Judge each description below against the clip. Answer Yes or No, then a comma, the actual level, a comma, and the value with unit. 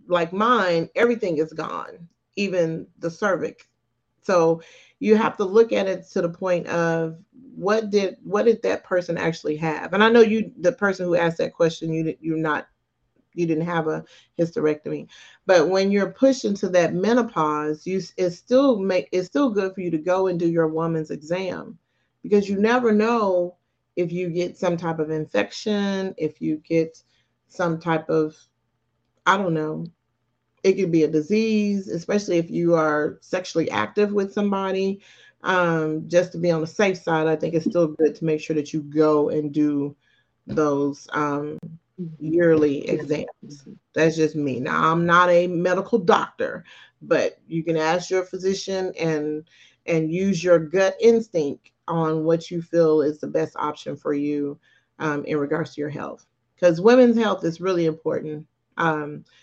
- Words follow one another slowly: No, average, 175 wpm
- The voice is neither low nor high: Yes, medium, 170 Hz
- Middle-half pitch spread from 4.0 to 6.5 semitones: No, average, 3.5 semitones